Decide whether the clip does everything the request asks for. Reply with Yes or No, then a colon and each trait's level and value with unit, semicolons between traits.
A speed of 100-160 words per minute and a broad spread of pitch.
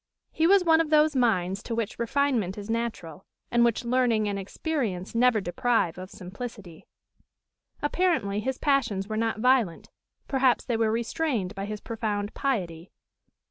No: average, 150 wpm; average, 4.6 semitones